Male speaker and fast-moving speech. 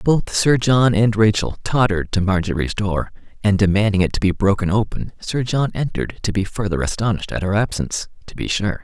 No: male; average, 195 wpm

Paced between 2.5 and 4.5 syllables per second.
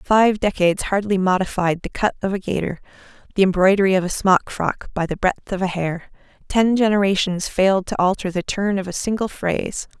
No: 5.5 syllables/s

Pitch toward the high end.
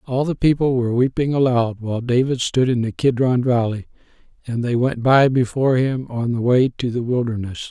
No: low, 125 Hz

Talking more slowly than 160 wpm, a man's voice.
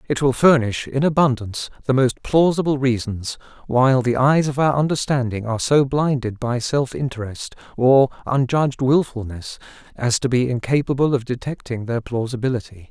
Yes: average, 150 wpm; male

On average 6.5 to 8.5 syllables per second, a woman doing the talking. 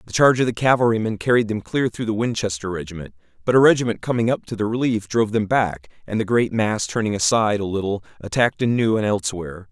No: 6.6 syllables/s; male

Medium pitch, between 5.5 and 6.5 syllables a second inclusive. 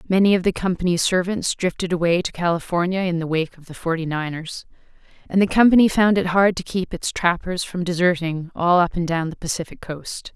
Yes: medium, 175 Hz; 5.6 syllables/s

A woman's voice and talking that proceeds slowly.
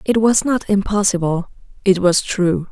Yes: female; slow, 130 wpm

